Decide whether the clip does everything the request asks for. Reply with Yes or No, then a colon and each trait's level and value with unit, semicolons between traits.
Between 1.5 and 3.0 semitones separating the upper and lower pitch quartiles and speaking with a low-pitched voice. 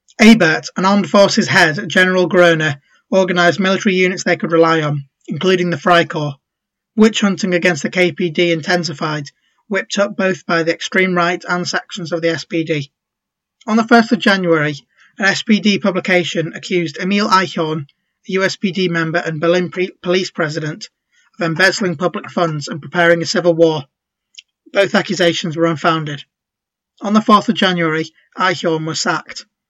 No: narrow, 2.5 semitones; medium, 180 Hz